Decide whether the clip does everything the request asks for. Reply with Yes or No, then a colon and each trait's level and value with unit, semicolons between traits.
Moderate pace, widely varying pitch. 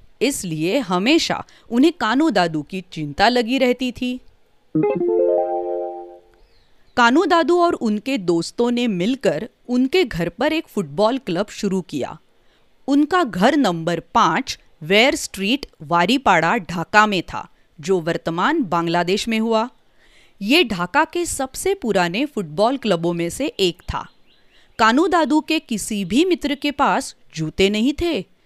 No: slow, 125 wpm; wide, 8.1 semitones